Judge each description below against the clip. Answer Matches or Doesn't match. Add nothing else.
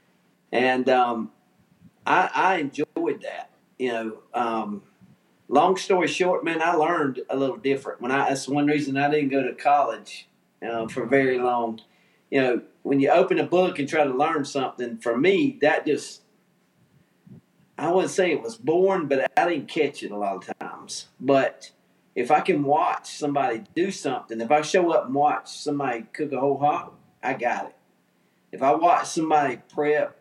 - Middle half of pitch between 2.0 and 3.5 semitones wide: Doesn't match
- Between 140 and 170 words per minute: Doesn't match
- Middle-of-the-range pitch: Matches